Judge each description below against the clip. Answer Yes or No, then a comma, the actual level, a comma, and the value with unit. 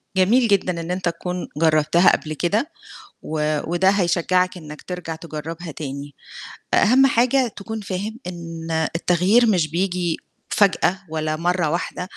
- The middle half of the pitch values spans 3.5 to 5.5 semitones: No, average, 3.1 semitones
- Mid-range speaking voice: Yes, medium, 175 Hz